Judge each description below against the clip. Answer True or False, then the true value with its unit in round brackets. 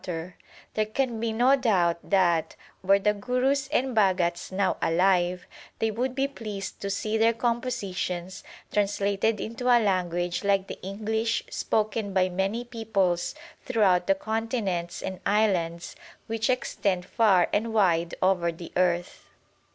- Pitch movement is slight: False (3.8 semitones)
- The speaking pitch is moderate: False (200 Hz)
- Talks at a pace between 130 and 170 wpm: True (150 wpm)